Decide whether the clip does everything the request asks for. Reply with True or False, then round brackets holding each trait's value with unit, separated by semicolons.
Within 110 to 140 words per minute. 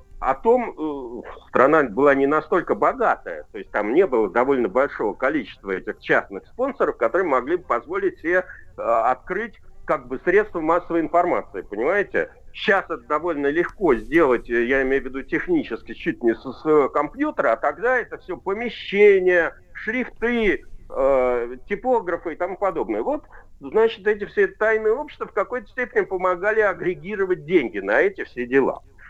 False (150 wpm)